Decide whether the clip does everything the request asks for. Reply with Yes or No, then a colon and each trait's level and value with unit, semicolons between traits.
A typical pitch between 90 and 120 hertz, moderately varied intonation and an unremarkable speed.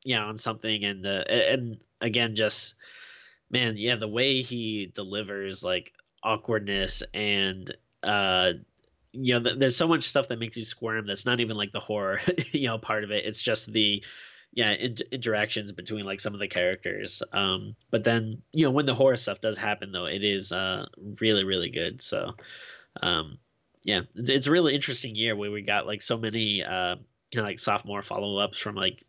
Yes: low, 110 Hz; average, 3.0 semitones; average, 190 wpm